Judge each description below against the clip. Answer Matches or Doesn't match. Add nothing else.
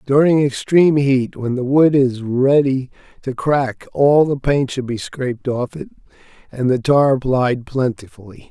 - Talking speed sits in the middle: Matches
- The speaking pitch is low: Matches